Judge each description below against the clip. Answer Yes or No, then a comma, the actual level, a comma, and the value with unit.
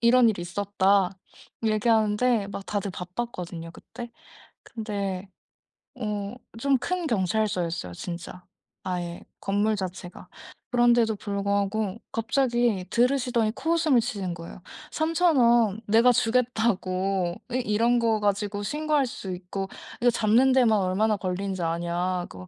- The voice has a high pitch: Yes, high, 210 Hz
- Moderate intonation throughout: Yes, average, 4.2 semitones